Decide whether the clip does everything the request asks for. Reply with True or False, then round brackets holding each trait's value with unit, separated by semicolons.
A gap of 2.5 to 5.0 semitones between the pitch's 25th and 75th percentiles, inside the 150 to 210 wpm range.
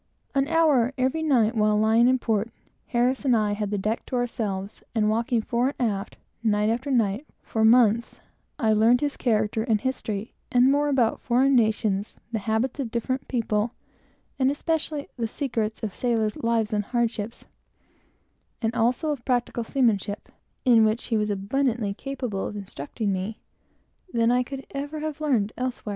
True (3.1 semitones; 170 wpm)